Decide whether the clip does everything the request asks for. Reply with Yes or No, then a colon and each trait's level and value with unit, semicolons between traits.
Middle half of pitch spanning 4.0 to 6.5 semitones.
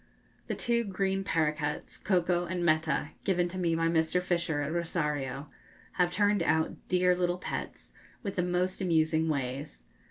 No: narrow, 2.5 semitones